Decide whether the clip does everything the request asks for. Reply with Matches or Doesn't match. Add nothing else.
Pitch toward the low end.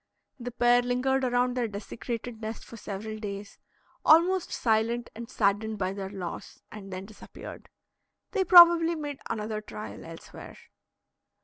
Doesn't match